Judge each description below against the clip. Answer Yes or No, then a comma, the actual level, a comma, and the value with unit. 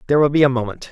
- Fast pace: Yes, fast, 330 wpm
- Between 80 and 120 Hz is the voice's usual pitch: No, low, 135 Hz